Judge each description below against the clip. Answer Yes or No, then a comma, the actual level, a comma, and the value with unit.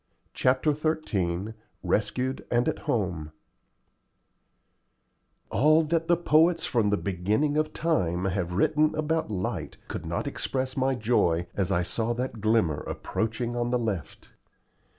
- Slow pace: Yes, slow, 130 wpm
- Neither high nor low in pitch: No, low, 120 Hz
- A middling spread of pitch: No, wide, 7.7 semitones